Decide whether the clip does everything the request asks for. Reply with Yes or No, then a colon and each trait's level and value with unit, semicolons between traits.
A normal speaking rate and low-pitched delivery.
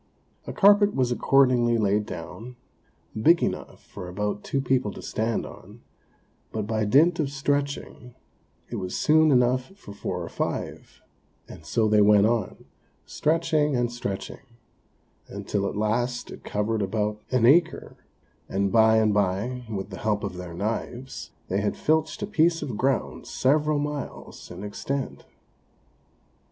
Yes: average, 145 wpm; low, 120 Hz